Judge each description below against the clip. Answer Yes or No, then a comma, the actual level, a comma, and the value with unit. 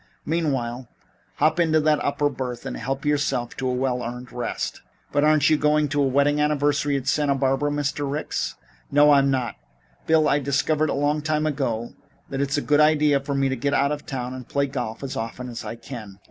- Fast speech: Yes, fast, 210 wpm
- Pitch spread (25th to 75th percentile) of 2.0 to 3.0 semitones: Yes, narrow, 2.5 semitones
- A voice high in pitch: No, medium, 140 Hz